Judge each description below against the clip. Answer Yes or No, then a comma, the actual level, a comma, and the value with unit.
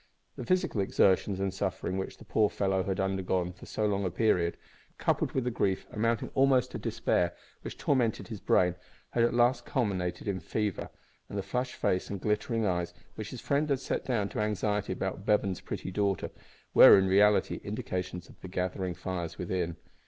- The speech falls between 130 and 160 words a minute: No, average, 185 wpm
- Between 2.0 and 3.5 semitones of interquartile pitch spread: Yes, average, 3.0 semitones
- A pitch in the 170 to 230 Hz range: No, low, 100 Hz